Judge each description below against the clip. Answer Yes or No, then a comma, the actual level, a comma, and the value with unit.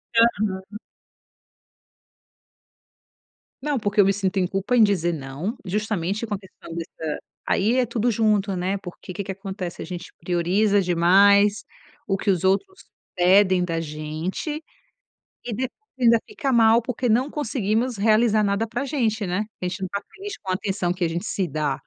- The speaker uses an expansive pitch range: No, average, 3.7 semitones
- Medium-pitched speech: No, high, 200 Hz